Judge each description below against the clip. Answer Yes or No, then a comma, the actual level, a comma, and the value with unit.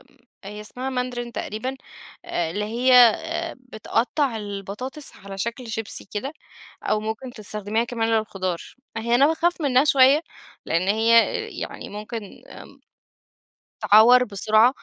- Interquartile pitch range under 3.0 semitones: No, average, 3.5 semitones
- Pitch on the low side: No, high, 230 Hz